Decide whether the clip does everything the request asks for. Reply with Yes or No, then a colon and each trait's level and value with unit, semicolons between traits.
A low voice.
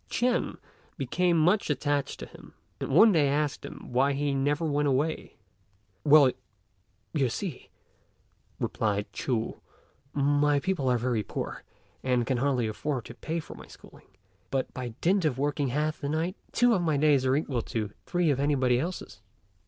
No: medium, 145 Hz